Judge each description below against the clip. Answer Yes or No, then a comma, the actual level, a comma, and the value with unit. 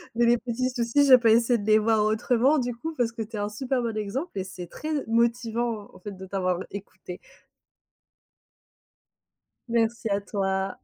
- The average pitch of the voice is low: No, high, 230 Hz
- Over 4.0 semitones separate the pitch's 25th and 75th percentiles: No, average, 2.9 semitones